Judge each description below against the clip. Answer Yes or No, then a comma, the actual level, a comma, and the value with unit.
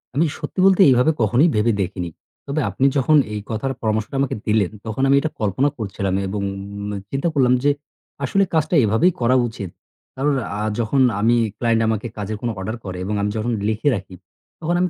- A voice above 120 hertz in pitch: No, low, 115 Hz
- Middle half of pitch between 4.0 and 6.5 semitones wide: Yes, average, 4.8 semitones